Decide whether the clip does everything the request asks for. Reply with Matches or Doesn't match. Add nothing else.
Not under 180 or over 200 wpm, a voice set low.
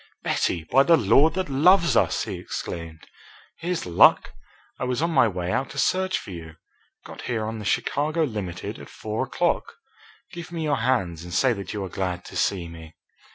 Matches